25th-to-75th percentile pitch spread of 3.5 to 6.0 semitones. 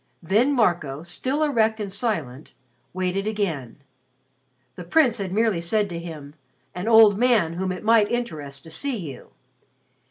Yes: average, 5.1 semitones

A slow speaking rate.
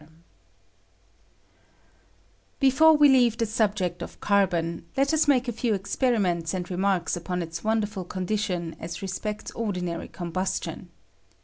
Yes: slow, 125 wpm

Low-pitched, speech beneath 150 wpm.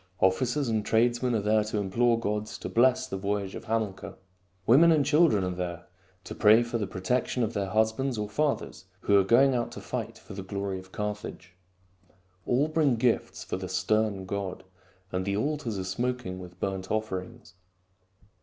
No: low, 110 Hz; average, 180 wpm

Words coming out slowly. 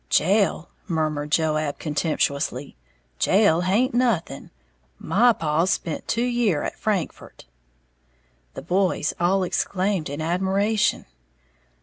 Yes: slow, 100 wpm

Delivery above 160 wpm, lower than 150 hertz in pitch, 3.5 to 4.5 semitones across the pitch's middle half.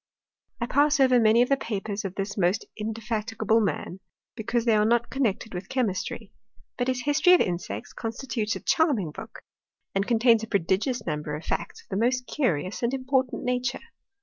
No: average, 180 wpm; high, 225 Hz; average, 4.1 semitones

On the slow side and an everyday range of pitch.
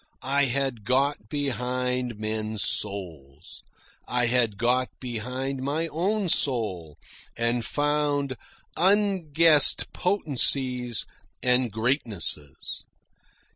Yes: slow, 85 wpm; average, 4.4 semitones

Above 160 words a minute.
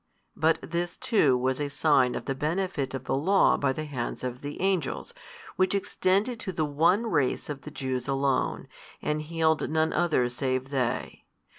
Yes: average, 170 wpm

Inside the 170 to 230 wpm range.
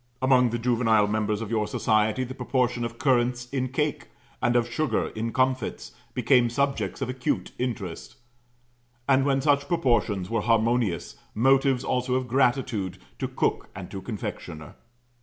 No: average, 150 wpm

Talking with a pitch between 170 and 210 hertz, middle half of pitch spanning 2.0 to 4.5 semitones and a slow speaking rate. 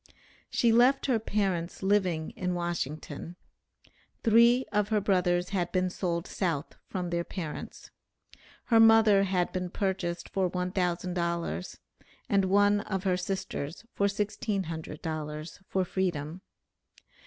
Yes: medium, 185 Hz; average, 2.8 semitones; slow, 120 wpm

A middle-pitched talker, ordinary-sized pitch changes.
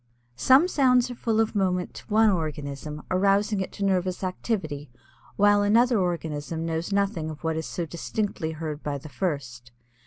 Yes: medium, 180 Hz; average, 4.8 semitones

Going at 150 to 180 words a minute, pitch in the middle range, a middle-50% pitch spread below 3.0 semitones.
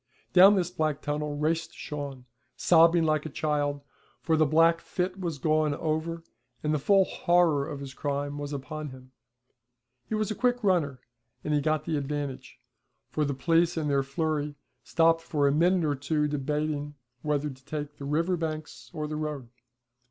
Yes: average, 175 wpm; medium, 150 Hz; narrow, 2.4 semitones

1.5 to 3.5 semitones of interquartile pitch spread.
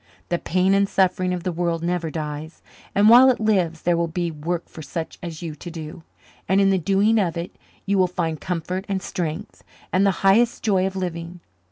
Yes: average, 2.7 semitones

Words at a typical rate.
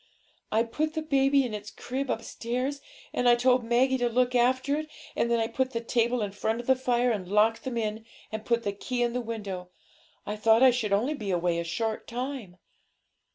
No: fast, 215 wpm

